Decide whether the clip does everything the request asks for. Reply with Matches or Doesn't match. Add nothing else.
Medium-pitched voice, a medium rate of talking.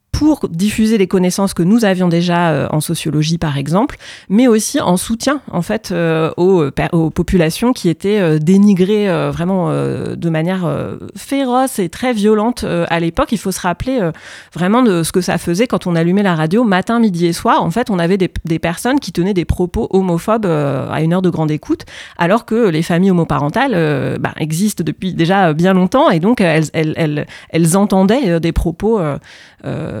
Matches